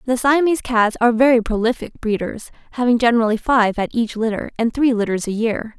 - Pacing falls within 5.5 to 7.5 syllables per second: Yes, 6.0 syllables/s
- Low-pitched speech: No, high, 230 Hz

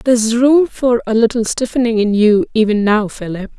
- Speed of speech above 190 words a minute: No, average, 185 wpm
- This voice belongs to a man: No, female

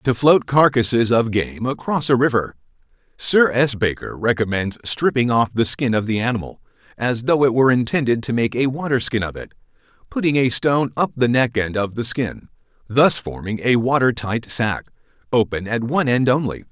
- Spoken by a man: Yes, male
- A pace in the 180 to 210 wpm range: Yes, average, 185 wpm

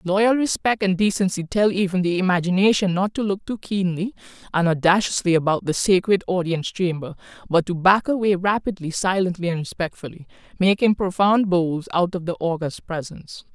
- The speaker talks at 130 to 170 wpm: Yes, average, 160 wpm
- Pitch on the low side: No, medium, 185 Hz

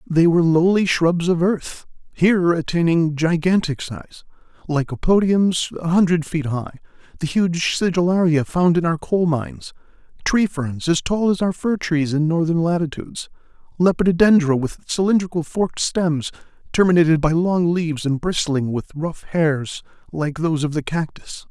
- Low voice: No, medium, 165 Hz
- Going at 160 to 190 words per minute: No, average, 150 wpm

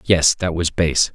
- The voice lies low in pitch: Yes, very low, 85 Hz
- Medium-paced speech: No, fast, 210 wpm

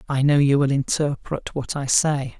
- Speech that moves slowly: No, average, 200 wpm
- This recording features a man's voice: Yes, male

